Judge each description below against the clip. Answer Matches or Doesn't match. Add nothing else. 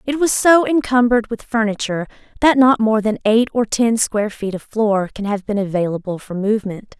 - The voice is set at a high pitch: Matches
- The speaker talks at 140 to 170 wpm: Doesn't match